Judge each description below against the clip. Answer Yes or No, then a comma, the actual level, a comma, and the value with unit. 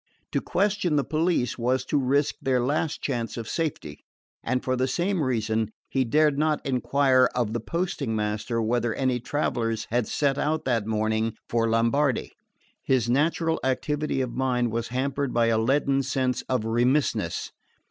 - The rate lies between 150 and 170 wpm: Yes, average, 160 wpm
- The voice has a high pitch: No, low, 130 Hz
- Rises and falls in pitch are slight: No, average, 3.7 semitones